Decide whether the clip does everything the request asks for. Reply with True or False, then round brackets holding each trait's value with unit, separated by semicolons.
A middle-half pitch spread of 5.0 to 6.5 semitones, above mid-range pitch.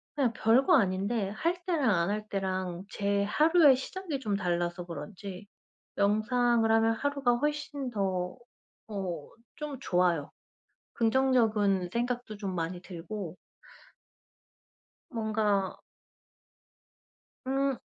True (5.5 semitones; 215 Hz)